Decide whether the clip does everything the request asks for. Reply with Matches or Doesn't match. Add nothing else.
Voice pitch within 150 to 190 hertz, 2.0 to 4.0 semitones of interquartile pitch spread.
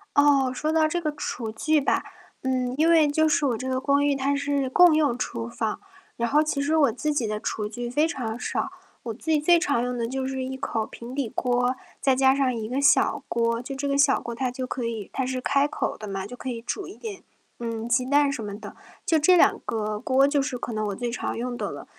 Doesn't match